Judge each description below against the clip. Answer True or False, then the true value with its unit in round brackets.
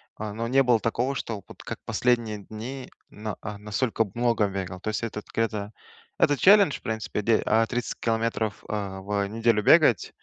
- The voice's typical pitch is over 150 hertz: False (110 Hz)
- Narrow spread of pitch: True (2.2 semitones)